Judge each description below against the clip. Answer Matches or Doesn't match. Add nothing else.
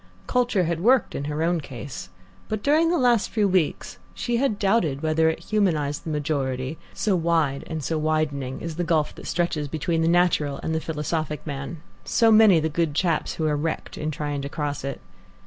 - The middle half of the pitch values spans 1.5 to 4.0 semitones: Matches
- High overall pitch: Doesn't match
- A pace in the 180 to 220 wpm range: Matches